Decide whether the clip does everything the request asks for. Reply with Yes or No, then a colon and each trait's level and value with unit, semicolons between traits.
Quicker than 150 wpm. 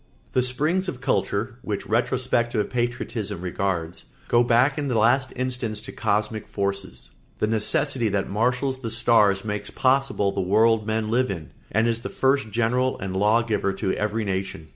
Yes: average, 170 wpm